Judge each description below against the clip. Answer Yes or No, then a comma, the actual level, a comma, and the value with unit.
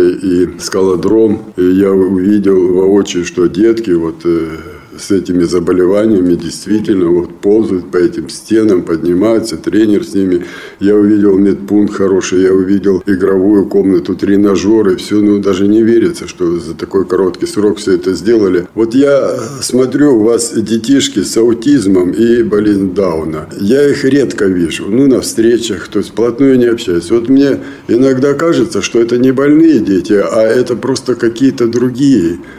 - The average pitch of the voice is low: Yes, low, 105 Hz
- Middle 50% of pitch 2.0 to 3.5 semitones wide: No, average, 4.7 semitones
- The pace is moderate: Yes, average, 150 wpm